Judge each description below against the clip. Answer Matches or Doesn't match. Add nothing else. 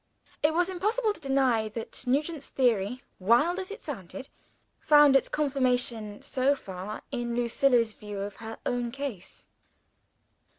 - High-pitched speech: Matches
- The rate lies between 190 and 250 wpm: Doesn't match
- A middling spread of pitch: Matches